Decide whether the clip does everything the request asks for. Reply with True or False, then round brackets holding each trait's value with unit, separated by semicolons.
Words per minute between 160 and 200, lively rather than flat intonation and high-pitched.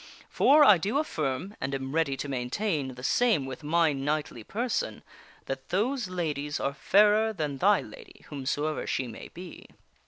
False (165 wpm; 7.3 semitones; 155 Hz)